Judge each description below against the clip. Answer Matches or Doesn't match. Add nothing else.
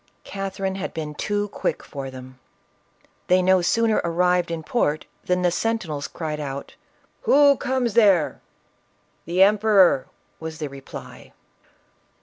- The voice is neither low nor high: Matches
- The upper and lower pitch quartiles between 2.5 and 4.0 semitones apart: Doesn't match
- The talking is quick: Doesn't match